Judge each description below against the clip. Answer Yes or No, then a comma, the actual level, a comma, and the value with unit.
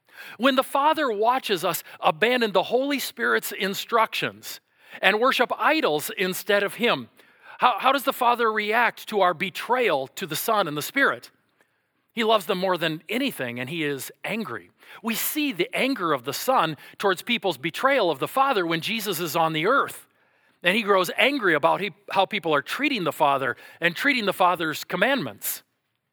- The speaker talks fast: No, average, 175 wpm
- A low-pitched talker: No, high, 200 Hz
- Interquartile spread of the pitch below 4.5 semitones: No, wide, 5.6 semitones